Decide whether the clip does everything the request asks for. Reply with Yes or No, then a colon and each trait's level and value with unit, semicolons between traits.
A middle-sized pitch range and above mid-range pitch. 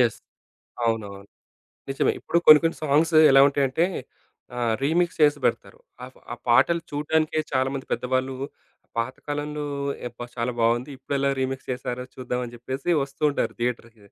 No: average, 3.3 semitones; low, 130 Hz